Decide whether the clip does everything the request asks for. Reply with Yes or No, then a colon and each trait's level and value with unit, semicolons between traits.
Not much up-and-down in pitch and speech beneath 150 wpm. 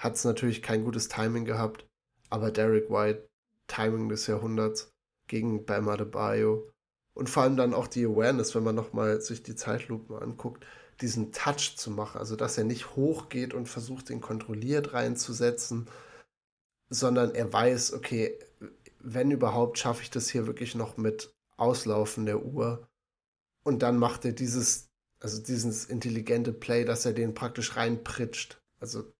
No: narrow, 1.9 semitones; average, 155 wpm